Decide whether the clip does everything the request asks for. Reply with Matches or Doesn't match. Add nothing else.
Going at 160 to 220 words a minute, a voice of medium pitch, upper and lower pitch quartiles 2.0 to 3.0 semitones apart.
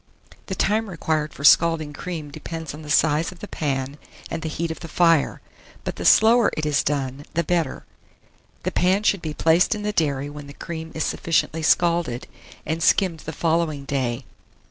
Matches